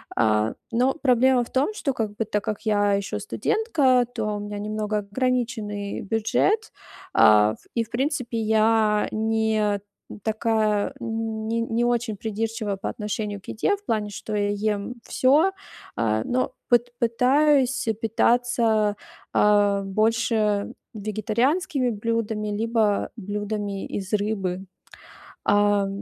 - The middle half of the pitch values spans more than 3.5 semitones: No, narrow, 2.6 semitones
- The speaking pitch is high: Yes, high, 220 Hz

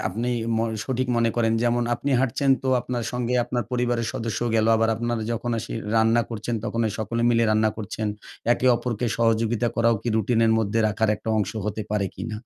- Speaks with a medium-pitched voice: No, low, 115 Hz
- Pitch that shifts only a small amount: Yes, narrow, 1.5 semitones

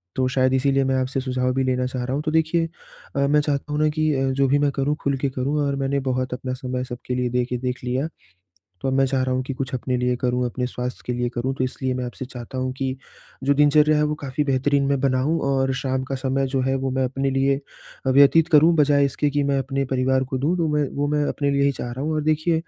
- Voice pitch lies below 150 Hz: Yes, low, 135 Hz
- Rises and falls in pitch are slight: Yes, narrow, 1.8 semitones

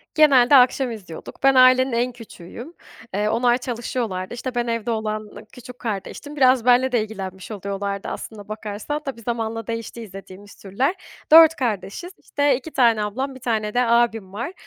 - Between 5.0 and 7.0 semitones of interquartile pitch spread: No, average, 3.4 semitones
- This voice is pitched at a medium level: No, high, 235 Hz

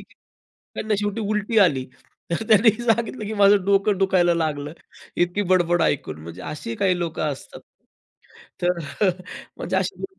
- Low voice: No, high, 195 Hz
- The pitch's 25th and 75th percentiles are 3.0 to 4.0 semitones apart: Yes, average, 3.6 semitones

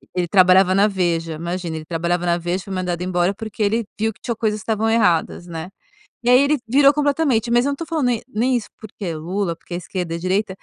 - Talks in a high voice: Yes, high, 195 Hz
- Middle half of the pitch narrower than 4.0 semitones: No, average, 4.6 semitones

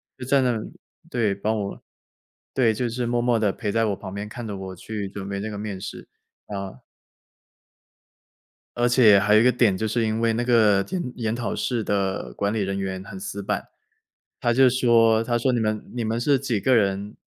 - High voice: No, low, 110 Hz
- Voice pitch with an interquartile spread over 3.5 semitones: No, average, 3.1 semitones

